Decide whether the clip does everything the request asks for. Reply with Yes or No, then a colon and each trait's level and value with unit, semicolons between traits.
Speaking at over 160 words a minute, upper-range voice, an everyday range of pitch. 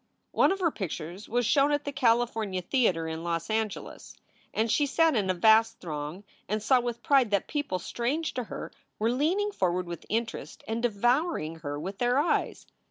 No: average, 185 wpm; high, 225 Hz; wide, 6.4 semitones